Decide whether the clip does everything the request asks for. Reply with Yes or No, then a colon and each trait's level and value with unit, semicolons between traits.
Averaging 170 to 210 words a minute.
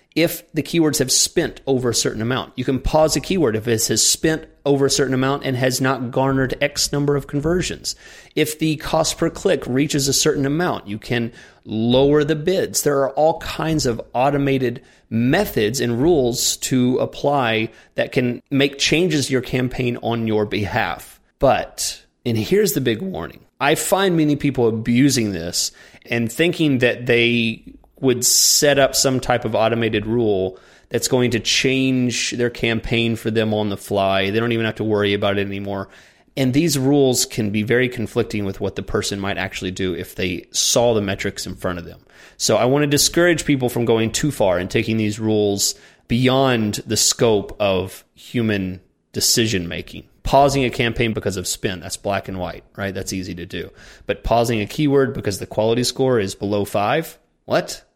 Yes: average, 185 wpm